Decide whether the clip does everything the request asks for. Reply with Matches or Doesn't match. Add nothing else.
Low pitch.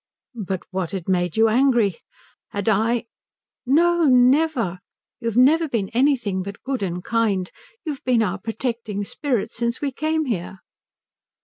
Doesn't match